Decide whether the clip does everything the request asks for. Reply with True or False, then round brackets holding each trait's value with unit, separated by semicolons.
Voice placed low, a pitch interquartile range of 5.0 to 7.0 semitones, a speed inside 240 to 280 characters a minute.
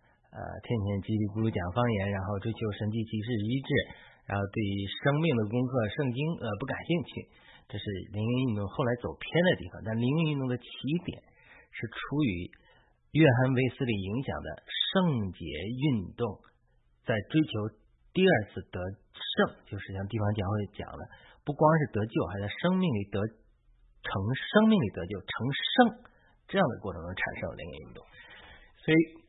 True (115 Hz; 5.6 semitones; 245 characters per minute)